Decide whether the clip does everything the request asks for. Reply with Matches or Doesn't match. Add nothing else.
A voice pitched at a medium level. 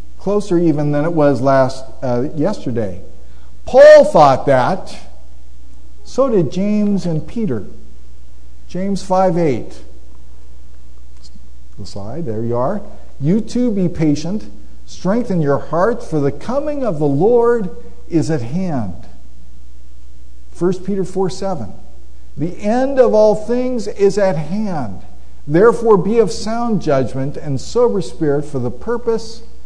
Matches